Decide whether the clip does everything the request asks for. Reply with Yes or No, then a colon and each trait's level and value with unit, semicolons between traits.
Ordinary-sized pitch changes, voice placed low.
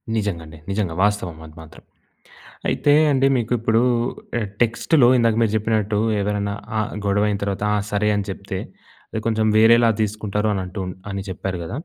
No: narrow, 2.2 semitones; low, 105 Hz